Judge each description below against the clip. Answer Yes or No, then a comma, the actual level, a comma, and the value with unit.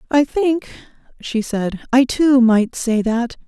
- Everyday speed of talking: Yes, average, 155 wpm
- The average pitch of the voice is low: No, very high, 250 Hz